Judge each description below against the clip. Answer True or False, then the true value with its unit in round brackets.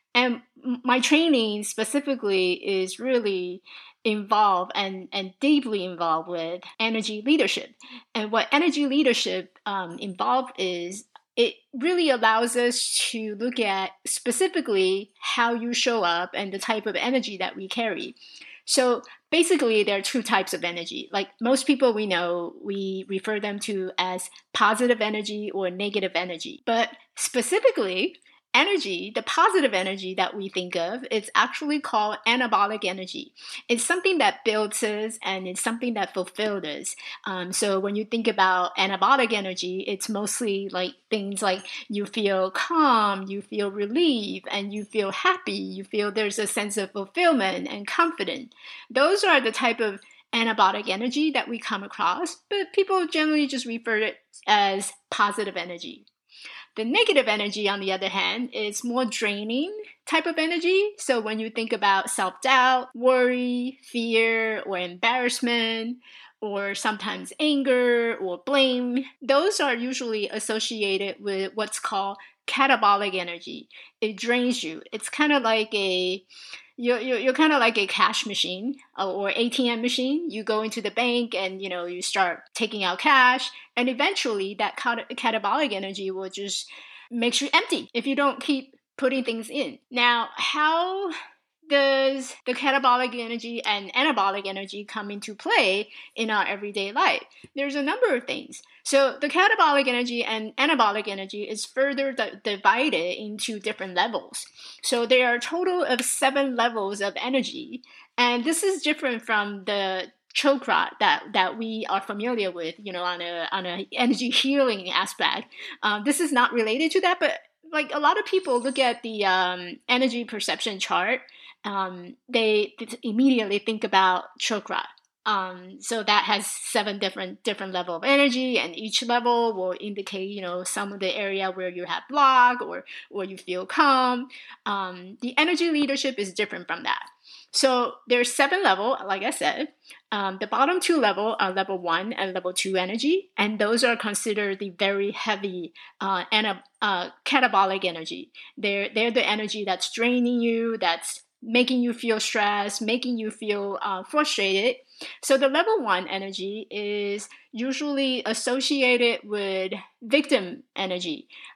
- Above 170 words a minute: False (155 wpm)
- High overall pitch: True (225 Hz)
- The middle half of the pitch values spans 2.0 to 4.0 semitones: False (4.9 semitones)